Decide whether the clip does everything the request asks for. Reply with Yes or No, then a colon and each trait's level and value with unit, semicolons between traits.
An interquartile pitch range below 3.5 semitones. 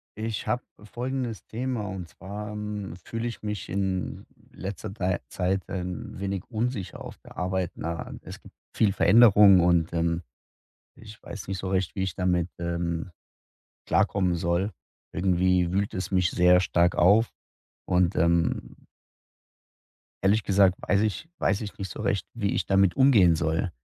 Yes: average, 2.9 semitones